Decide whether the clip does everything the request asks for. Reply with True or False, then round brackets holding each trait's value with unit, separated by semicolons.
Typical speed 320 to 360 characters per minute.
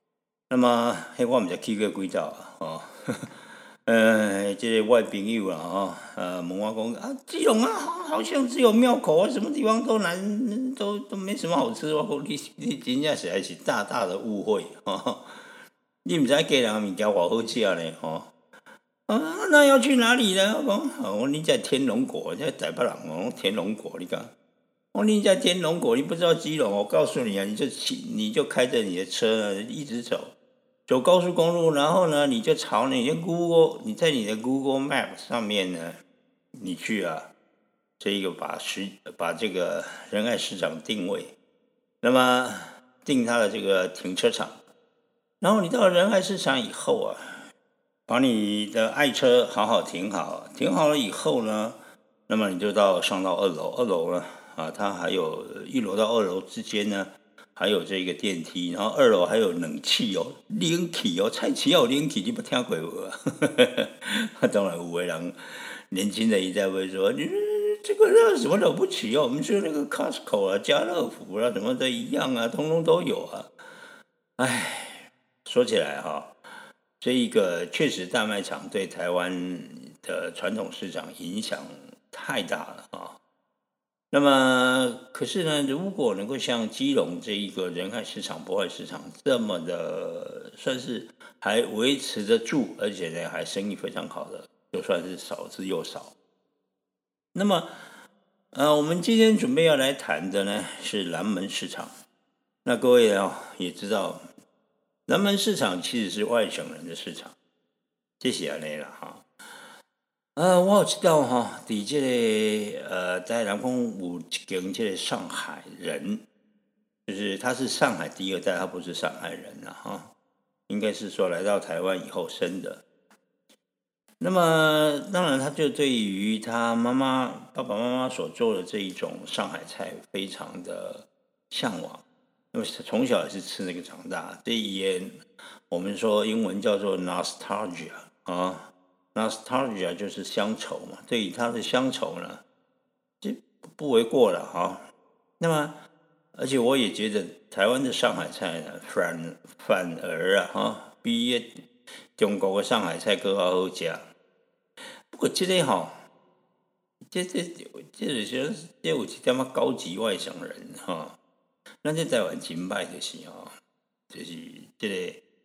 False (240 characters per minute)